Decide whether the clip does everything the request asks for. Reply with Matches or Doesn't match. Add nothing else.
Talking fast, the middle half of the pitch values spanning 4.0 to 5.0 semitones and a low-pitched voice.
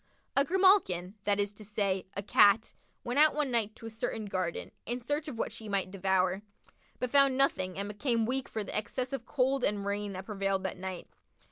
Doesn't match